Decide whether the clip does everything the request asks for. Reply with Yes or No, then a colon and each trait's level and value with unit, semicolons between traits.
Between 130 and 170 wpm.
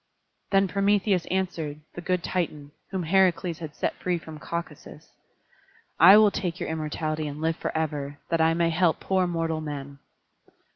Yes: average, 155 wpm